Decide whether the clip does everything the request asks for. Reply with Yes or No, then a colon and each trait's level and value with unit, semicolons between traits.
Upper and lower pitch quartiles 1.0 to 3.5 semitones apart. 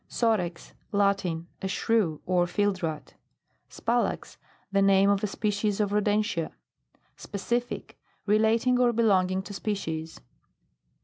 Yes: average, 2.8 semitones